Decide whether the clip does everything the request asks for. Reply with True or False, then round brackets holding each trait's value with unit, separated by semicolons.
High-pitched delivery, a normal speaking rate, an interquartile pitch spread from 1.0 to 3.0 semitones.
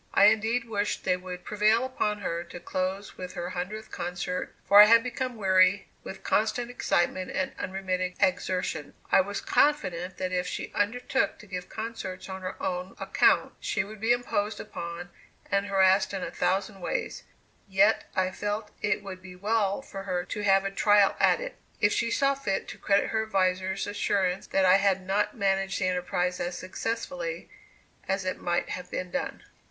True (195 Hz; 180 wpm; 2.4 semitones)